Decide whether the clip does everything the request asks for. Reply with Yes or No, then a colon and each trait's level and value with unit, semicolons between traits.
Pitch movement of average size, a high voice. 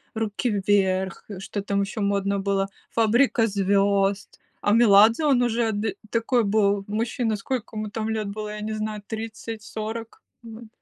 No: narrow, 2.0 semitones; high, 215 Hz